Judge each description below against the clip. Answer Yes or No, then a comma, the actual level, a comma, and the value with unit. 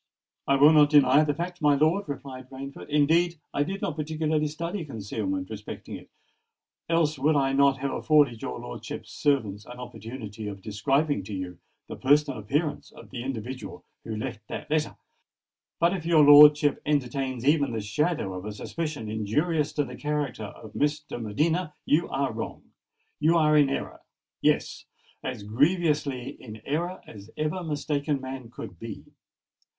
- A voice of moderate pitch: Yes, medium, 145 Hz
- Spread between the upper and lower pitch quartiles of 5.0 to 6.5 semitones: No, average, 4.2 semitones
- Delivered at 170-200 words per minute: No, average, 155 wpm